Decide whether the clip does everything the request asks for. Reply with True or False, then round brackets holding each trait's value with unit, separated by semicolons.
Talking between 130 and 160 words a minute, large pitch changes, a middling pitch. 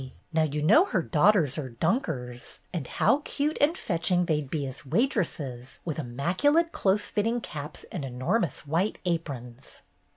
True (155 wpm; 7.2 semitones; 160 Hz)